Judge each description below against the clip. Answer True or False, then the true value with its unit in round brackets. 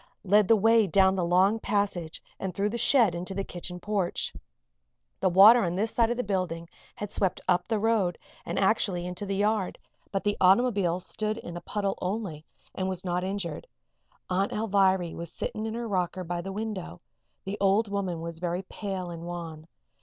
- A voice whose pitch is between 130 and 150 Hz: False (190 Hz)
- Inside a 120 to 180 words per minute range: False (190 wpm)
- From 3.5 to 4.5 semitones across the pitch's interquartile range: False (2.8 semitones)